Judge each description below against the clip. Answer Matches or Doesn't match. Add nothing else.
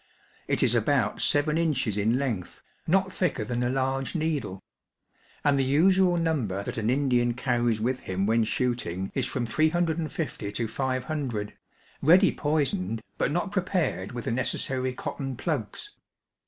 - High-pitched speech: Doesn't match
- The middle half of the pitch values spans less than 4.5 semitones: Doesn't match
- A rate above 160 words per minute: Doesn't match